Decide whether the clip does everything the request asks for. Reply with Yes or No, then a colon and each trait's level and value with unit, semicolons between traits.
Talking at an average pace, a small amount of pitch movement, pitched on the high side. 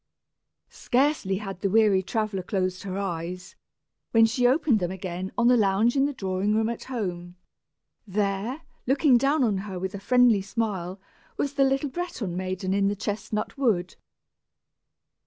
No: average, 155 wpm; average, 4.5 semitones; high, 205 Hz